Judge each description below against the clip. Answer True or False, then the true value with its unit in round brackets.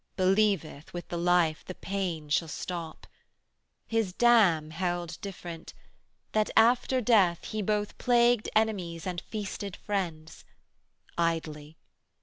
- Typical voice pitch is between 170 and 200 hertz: True (185 Hz)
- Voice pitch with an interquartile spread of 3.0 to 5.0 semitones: True (4.3 semitones)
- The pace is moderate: False (120 wpm)